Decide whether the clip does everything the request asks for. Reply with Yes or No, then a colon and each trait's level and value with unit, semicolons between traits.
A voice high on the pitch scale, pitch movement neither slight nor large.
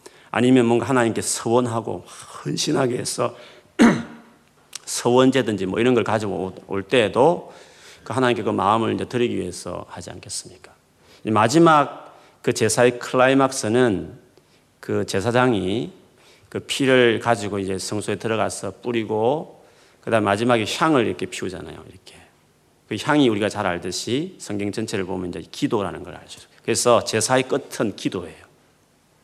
No: low, 115 Hz; average, 3.4 semitones